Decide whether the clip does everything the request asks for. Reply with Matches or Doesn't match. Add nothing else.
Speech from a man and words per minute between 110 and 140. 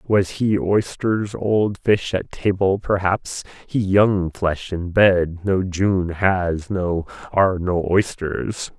Matches